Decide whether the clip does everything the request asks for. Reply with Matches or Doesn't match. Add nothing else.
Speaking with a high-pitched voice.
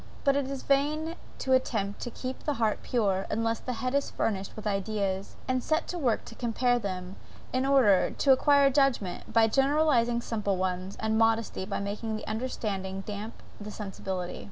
Matches